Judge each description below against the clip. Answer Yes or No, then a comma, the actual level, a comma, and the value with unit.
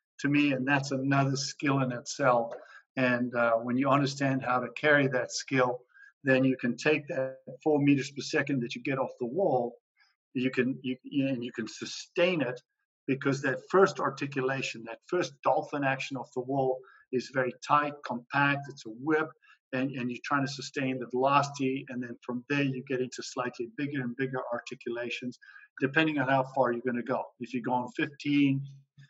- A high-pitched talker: No, low, 135 Hz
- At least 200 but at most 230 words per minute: No, average, 185 wpm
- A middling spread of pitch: No, narrow, 2.2 semitones